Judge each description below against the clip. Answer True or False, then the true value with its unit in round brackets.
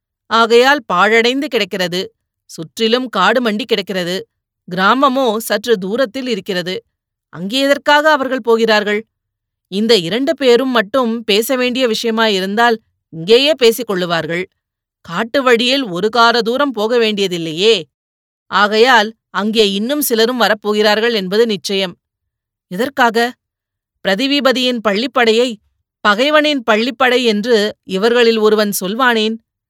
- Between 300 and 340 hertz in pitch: False (225 Hz)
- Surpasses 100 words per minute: False (95 wpm)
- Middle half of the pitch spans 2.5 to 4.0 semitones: True (3.7 semitones)